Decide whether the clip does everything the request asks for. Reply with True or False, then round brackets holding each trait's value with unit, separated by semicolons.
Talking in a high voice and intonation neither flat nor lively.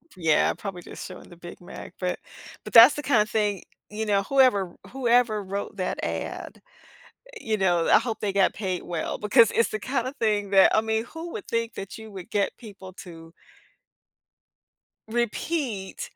True (210 Hz; 3.6 semitones)